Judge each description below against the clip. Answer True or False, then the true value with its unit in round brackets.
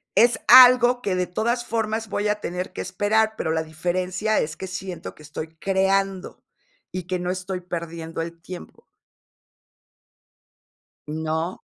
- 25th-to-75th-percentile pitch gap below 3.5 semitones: False (3.9 semitones)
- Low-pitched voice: False (185 Hz)